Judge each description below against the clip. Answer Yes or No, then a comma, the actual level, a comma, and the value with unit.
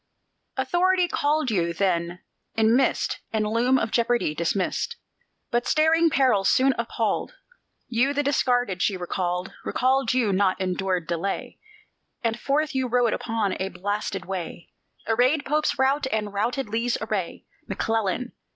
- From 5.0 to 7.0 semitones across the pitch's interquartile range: Yes, wide, 5.5 semitones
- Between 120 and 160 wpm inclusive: Yes, slow, 135 wpm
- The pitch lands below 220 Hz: No, high, 225 Hz